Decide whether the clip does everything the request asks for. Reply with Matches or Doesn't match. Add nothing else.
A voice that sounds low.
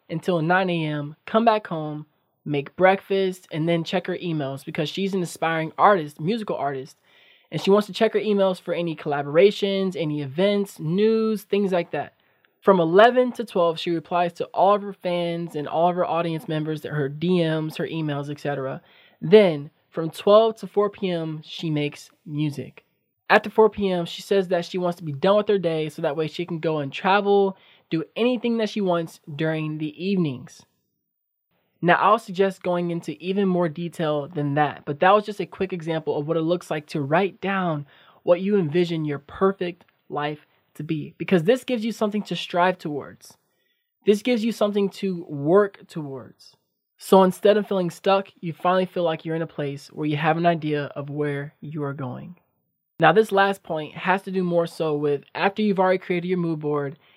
Doesn't match